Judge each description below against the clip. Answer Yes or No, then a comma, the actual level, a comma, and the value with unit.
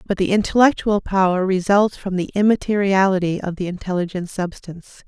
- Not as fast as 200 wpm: Yes, average, 140 wpm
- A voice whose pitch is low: No, high, 190 Hz